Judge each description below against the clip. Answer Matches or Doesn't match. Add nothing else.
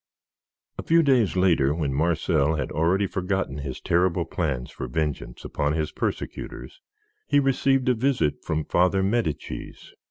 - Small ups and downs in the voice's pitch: Doesn't match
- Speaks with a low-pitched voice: Matches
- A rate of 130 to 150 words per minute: Matches